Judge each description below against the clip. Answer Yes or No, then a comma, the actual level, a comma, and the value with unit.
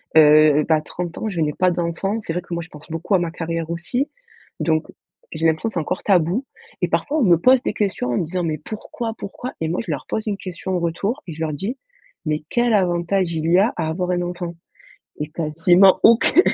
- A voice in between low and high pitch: Yes, medium, 175 Hz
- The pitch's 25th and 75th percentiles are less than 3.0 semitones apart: No, average, 3.5 semitones